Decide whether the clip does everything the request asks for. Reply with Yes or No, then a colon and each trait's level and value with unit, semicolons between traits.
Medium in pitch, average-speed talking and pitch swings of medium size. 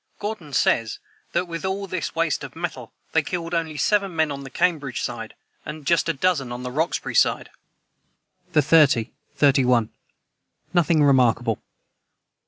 Yes: medium, 155 Hz; average, 150 wpm; average, 4.3 semitones